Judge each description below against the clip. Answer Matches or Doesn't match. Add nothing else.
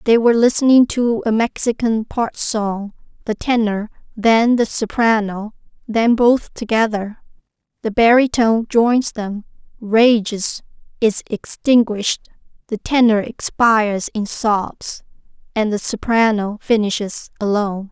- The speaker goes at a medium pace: Doesn't match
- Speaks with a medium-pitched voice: Doesn't match